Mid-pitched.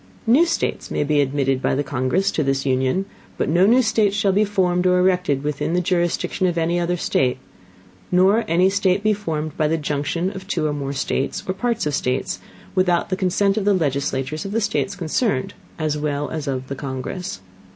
Yes: medium, 175 Hz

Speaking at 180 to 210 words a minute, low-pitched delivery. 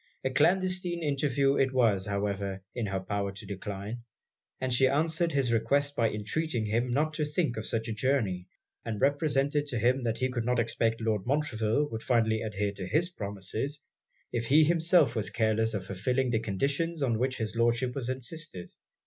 Yes: average, 185 wpm; low, 120 Hz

